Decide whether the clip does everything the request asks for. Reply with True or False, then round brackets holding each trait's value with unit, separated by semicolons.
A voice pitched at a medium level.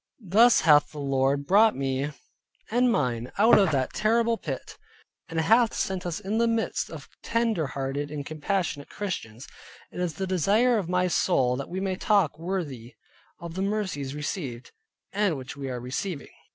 True (170 Hz)